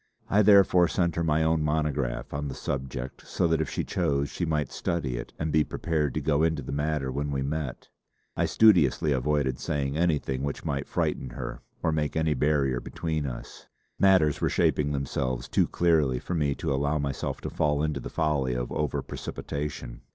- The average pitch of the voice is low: Yes, very low, 75 Hz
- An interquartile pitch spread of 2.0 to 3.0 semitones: Yes, narrow, 2.6 semitones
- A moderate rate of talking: Yes, average, 190 wpm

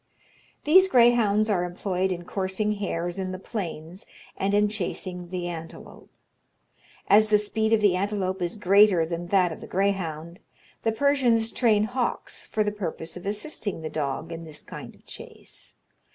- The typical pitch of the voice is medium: No, high, 195 Hz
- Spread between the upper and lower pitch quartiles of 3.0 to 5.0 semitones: Yes, average, 3.5 semitones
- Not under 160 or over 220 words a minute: Yes, average, 165 wpm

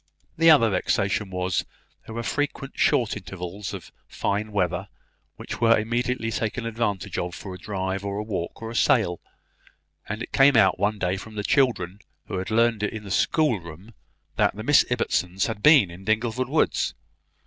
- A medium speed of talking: Yes, average, 180 wpm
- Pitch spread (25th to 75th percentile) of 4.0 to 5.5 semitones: No, average, 3.5 semitones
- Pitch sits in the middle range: No, low, 105 Hz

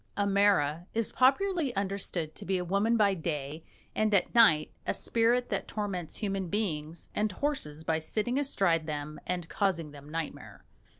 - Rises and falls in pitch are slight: No, average, 5.3 semitones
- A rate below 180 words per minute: Yes, average, 165 wpm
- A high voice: Yes, high, 195 Hz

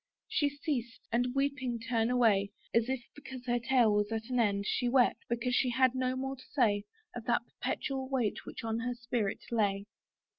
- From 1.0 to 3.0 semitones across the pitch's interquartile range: Yes, narrow, 2.4 semitones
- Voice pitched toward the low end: No, high, 245 Hz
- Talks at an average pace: Yes, average, 190 wpm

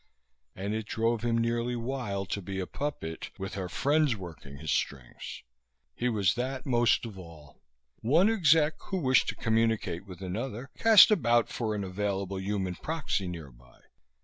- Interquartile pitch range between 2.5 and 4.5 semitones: No, average, 5.2 semitones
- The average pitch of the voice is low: Yes, low, 110 Hz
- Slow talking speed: No, average, 160 wpm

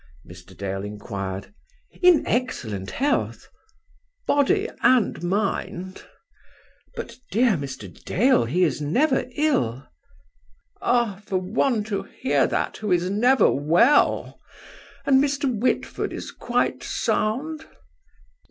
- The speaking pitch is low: No, high, 205 Hz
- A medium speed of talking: No, slow, 105 wpm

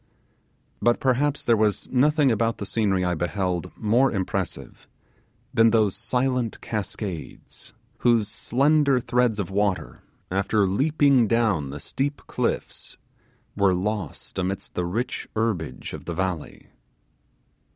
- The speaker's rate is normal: No, slow, 120 wpm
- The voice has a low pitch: Yes, low, 110 Hz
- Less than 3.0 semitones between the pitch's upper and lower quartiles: No, average, 4.7 semitones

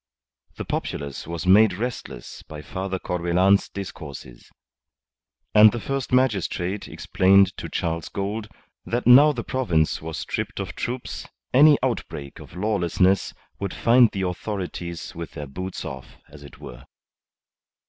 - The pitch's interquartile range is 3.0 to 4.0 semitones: No, average, 4.8 semitones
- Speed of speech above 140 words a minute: No, slow, 135 wpm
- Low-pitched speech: Yes, very low, 95 Hz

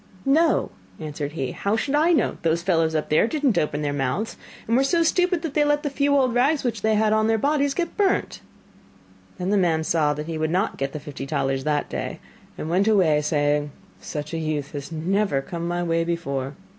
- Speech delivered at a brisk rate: Yes, fast, 220 wpm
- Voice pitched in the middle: Yes, medium, 170 Hz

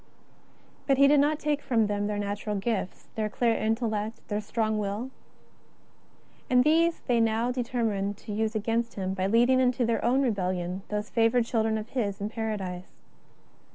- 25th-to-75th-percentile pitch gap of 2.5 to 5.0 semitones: Yes, average, 3.0 semitones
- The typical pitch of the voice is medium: No, high, 220 Hz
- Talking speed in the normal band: Yes, average, 165 wpm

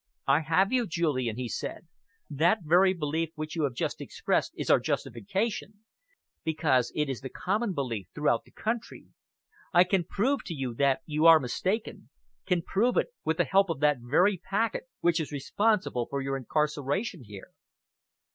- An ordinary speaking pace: Yes, average, 170 wpm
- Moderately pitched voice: Yes, medium, 160 Hz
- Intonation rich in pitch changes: Yes, wide, 5.9 semitones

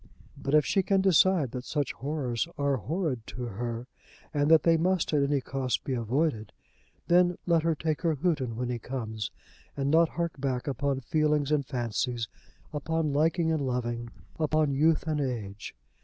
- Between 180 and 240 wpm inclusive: No, average, 170 wpm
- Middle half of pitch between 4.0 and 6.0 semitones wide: Yes, average, 4.3 semitones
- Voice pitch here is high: No, medium, 140 Hz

